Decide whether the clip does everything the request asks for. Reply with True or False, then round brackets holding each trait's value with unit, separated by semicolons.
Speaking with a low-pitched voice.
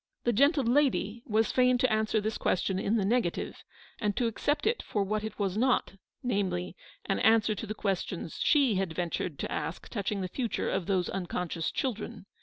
False (215 Hz)